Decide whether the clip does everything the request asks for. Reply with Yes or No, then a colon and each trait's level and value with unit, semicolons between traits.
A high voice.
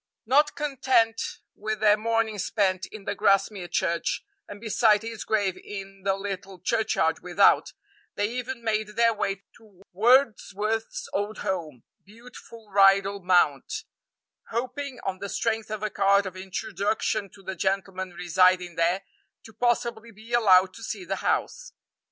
Yes: high, 205 Hz